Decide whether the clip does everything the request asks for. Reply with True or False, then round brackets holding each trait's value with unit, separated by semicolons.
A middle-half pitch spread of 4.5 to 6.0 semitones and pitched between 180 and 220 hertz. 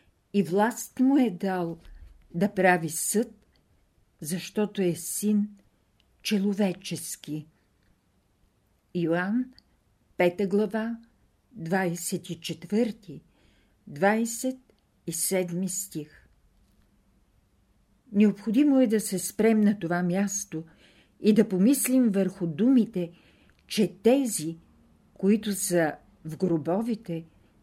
True (5.0 semitones; 185 Hz)